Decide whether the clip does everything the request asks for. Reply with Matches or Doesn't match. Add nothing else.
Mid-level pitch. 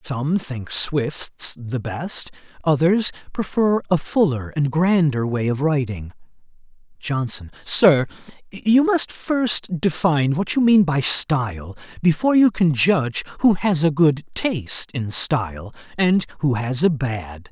Matches